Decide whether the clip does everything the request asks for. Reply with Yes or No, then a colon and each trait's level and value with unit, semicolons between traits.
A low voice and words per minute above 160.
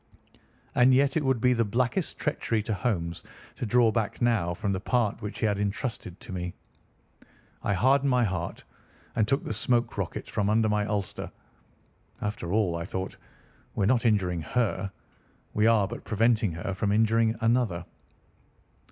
Yes: low, 110 Hz; average, 170 wpm